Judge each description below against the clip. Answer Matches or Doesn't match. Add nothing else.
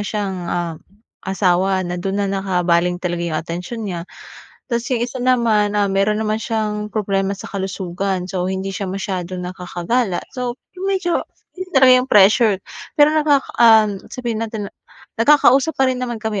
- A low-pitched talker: Doesn't match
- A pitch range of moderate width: Matches